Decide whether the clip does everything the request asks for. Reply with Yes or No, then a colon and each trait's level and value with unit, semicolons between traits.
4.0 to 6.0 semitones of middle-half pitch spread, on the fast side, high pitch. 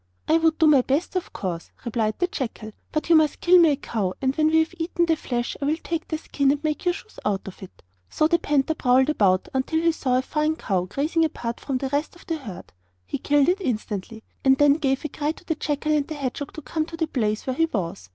Yes: average, 4.6 semitones; fast, 255 wpm; very high, 290 Hz